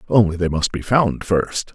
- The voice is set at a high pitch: No, very low, 95 Hz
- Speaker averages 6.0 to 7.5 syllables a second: No, 4.5 syllables/s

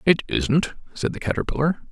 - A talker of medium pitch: Yes, medium, 150 Hz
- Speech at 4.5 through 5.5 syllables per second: Yes, 5.3 syllables/s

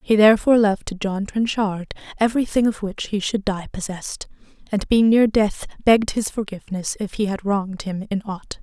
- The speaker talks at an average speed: Yes, average, 190 wpm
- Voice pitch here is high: Yes, high, 205 Hz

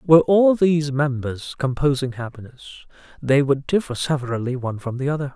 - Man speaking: Yes, male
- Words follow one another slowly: No, average, 155 wpm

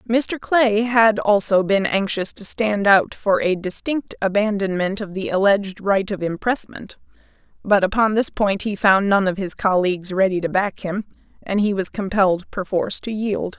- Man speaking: No, female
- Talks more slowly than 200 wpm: Yes, average, 175 wpm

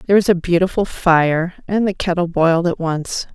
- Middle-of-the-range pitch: Yes, medium, 175 Hz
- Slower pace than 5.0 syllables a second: No, 5.3 syllables/s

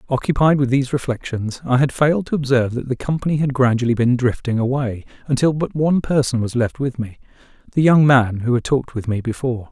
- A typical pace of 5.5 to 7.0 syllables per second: Yes, 6.2 syllables/s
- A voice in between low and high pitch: No, low, 130 Hz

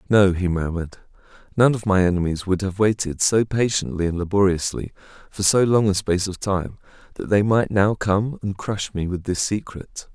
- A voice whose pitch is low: Yes, very low, 95 Hz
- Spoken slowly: No, average, 190 wpm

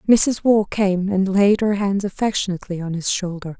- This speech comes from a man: No, female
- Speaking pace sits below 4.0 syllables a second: No, 5.1 syllables/s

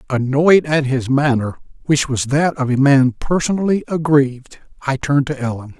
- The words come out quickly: No, average, 165 wpm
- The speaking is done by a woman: No, male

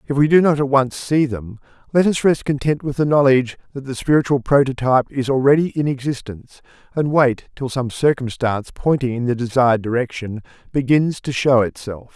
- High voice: No, low, 135 Hz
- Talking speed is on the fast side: No, average, 185 wpm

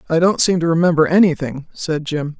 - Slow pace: No, average, 200 wpm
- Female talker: Yes, female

